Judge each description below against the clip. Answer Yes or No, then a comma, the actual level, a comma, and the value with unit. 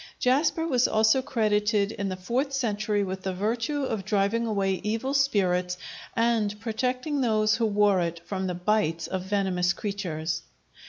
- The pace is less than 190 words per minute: Yes, average, 155 wpm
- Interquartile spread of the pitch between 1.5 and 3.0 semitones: No, average, 3.7 semitones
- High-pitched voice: Yes, high, 210 Hz